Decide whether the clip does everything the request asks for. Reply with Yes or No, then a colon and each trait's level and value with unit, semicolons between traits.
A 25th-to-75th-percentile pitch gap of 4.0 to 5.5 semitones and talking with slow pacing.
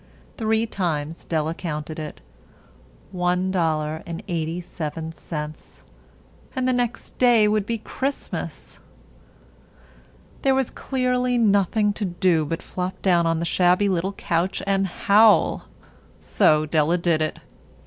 Yes: average, 4.7 semitones; slow, 130 wpm